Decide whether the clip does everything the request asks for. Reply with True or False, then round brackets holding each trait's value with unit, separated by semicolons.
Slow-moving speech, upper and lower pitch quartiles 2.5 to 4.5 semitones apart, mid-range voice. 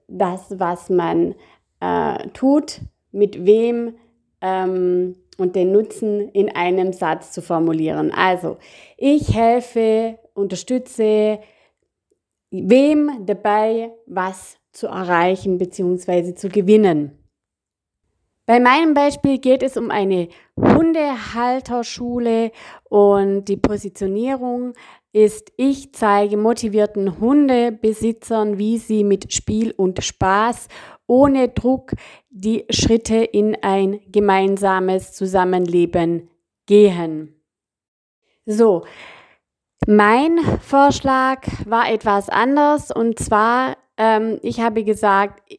False (95 wpm; 3.9 semitones; 210 Hz)